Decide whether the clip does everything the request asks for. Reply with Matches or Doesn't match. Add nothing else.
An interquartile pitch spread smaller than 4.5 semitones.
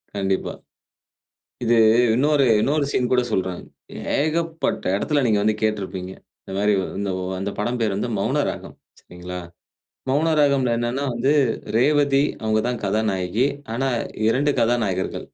Doesn't match